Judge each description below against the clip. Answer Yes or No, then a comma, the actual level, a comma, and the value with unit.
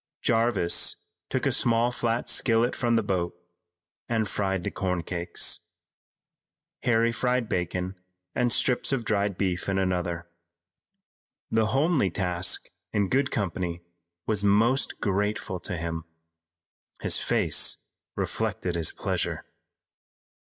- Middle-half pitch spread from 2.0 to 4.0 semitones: No, average, 4.6 semitones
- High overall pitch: No, low, 100 Hz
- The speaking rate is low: Yes, slow, 115 wpm